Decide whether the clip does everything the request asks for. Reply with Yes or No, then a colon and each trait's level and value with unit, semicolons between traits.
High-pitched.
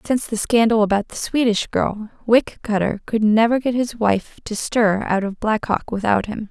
Yes: high, 220 Hz